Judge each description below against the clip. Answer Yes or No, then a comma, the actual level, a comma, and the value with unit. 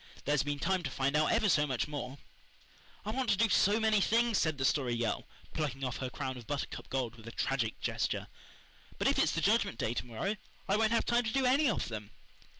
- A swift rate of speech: Yes, fast, 235 wpm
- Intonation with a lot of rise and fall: Yes, wide, 8.9 semitones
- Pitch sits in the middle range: Yes, medium, 150 Hz